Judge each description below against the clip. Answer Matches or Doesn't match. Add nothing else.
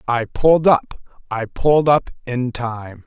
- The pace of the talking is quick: Doesn't match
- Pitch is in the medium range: Doesn't match